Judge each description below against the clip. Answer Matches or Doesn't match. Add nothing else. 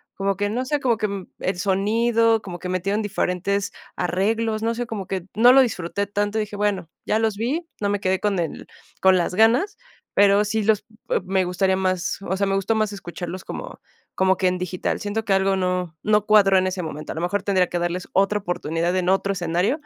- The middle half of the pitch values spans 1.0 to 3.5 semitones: Matches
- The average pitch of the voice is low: Doesn't match